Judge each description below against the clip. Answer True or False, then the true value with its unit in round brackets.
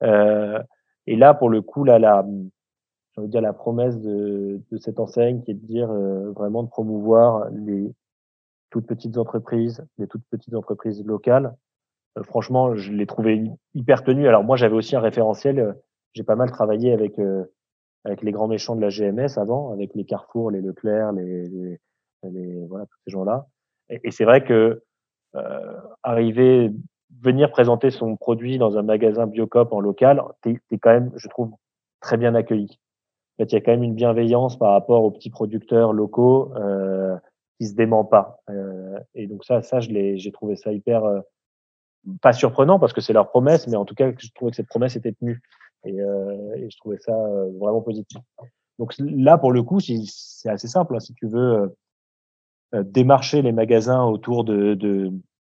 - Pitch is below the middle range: True (110 Hz)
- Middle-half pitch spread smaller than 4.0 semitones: True (2.8 semitones)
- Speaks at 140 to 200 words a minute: True (195 wpm)